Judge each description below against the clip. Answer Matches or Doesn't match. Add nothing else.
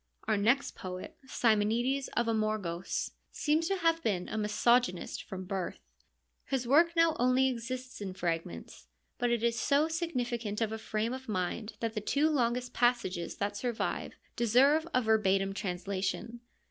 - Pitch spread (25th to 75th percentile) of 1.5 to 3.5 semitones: Doesn't match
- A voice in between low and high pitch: Doesn't match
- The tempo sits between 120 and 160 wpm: Matches